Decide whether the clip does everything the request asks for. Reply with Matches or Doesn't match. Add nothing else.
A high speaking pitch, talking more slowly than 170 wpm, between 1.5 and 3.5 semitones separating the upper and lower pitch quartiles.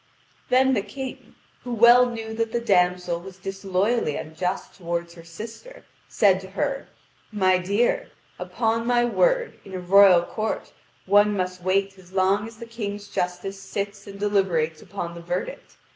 Doesn't match